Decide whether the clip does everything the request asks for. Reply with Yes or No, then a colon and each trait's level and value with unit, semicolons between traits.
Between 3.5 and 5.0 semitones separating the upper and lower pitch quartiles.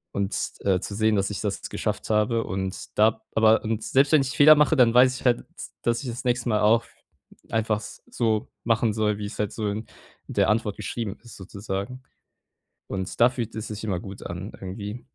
No: narrow, 2.5 semitones